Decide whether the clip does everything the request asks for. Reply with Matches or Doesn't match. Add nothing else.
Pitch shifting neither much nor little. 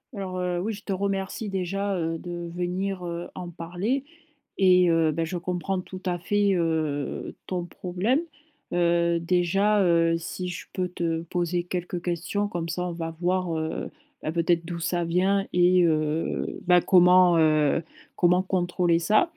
Doesn't match